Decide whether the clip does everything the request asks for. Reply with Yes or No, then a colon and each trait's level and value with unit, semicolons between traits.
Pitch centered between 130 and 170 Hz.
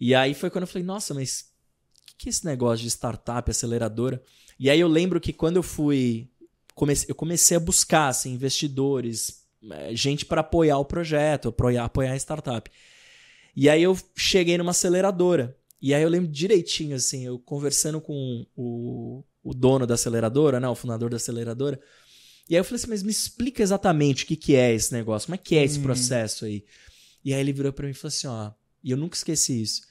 Yes: medium, 140 Hz